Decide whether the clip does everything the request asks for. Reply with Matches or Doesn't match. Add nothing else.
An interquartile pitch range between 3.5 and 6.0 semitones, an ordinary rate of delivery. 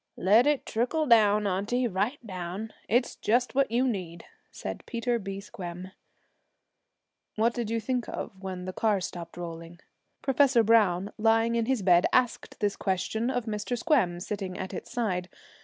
Matches